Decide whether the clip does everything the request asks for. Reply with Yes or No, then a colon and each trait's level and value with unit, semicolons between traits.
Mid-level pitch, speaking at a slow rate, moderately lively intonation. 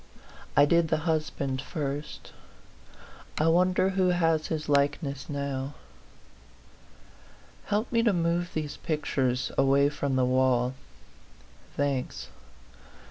Yes: medium, 145 Hz; slow, 105 wpm; average, 3.6 semitones